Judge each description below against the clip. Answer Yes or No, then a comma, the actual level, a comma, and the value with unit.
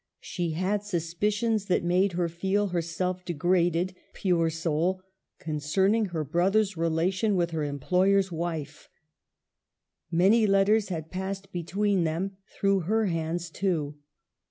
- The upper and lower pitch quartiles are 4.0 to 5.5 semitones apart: No, average, 2.9 semitones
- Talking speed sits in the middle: No, slow, 120 wpm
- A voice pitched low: No, medium, 180 Hz